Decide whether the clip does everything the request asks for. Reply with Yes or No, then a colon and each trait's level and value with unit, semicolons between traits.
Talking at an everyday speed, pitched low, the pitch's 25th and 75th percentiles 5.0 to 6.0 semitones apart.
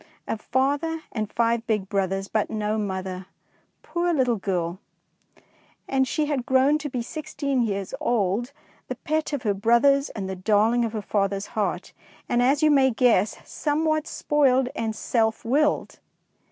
No: average, 155 wpm; high, 235 Hz; wide, 5.4 semitones